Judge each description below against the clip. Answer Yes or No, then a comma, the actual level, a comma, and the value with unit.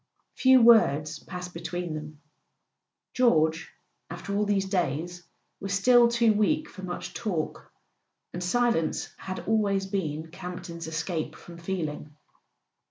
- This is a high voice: No, medium, 180 Hz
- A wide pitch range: No, average, 4.3 semitones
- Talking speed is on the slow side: Yes, slow, 120 wpm